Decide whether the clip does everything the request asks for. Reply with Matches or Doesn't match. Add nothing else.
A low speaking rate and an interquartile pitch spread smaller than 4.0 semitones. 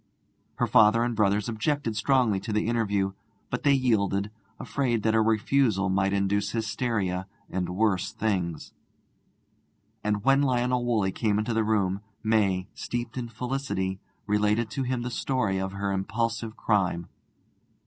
Doesn't match